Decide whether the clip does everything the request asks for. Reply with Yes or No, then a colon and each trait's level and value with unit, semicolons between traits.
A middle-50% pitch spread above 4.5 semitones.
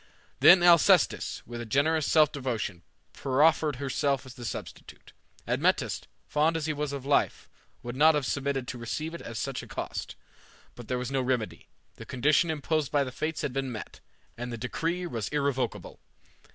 No: average, 3.7 semitones